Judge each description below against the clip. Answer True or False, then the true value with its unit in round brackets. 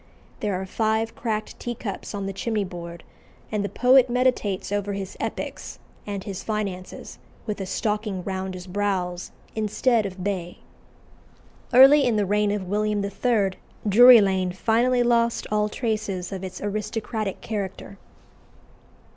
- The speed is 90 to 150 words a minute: True (140 wpm)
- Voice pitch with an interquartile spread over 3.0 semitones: False (2.6 semitones)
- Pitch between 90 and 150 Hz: False (205 Hz)